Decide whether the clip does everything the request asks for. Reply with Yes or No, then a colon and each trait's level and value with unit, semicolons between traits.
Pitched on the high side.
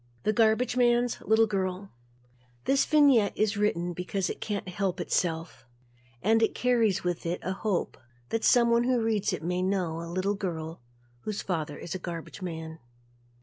Yes: high, 195 Hz